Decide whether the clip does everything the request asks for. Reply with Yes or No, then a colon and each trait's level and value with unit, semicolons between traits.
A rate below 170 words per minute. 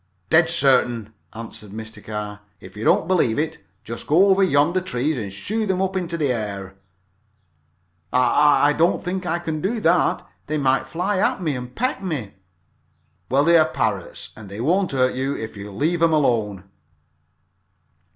No: average, 180 wpm